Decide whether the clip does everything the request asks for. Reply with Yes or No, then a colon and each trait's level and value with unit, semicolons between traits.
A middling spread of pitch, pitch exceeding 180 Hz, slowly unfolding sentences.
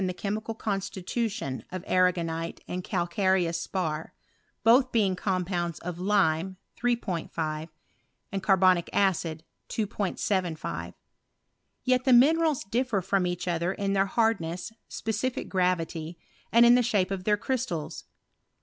Yes: average, 4.1 semitones; high, 190 Hz; slow, 130 wpm